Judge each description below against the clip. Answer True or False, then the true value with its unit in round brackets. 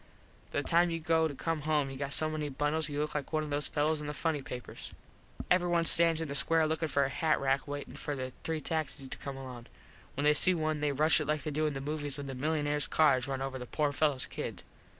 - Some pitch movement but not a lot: False (2.2 semitones)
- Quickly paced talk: True (260 wpm)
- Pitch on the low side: False (150 Hz)